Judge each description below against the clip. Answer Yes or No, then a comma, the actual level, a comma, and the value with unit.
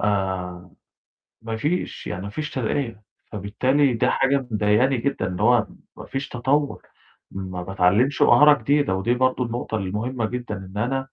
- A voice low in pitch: Yes, low, 115 Hz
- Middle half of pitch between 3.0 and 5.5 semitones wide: Yes, average, 5.0 semitones